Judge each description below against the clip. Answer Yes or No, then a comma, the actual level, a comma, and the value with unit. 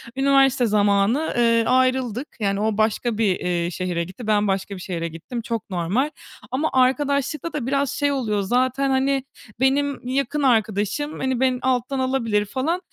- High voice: Yes, very high, 250 Hz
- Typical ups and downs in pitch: Yes, average, 4.6 semitones